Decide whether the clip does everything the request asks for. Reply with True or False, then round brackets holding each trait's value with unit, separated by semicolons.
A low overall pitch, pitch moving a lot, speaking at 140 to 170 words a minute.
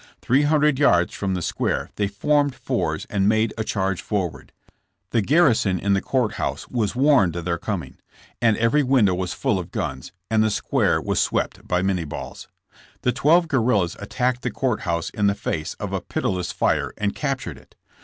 False (110 Hz; 5.8 semitones; 195 wpm)